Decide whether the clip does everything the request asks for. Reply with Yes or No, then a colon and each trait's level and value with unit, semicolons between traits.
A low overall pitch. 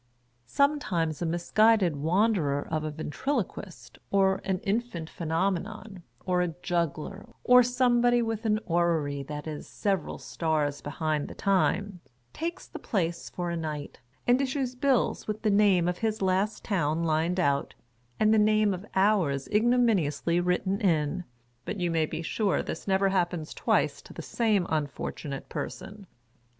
No: medium, 185 Hz